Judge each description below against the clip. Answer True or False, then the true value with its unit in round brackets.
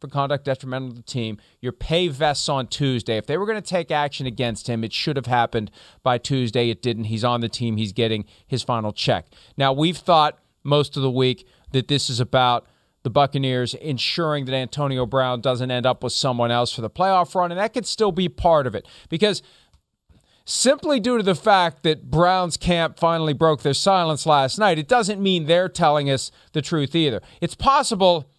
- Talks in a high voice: False (140 Hz)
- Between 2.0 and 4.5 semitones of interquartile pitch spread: False (5.1 semitones)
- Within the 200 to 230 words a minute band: True (205 wpm)